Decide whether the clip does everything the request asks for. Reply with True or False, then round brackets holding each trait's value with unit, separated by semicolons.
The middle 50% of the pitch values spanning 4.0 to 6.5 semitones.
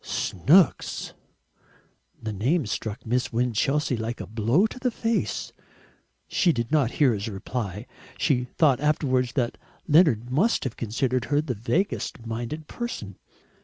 True (5.1 semitones)